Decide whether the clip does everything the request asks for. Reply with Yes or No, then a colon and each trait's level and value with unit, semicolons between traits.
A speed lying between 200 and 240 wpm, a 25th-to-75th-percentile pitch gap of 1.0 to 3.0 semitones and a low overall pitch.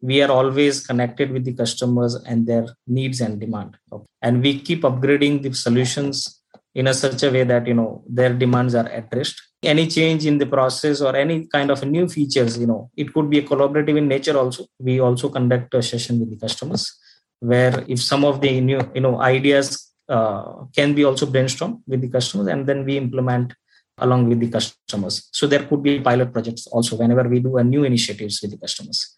Yes: fast, 205 wpm; narrow, 2.6 semitones; low, 130 Hz